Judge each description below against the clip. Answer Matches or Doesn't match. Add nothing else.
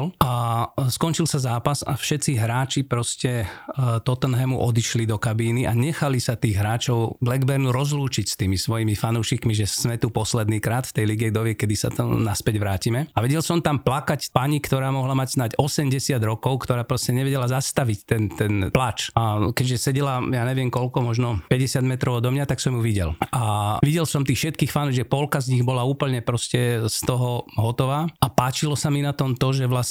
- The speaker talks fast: Matches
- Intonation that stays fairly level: Doesn't match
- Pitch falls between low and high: Doesn't match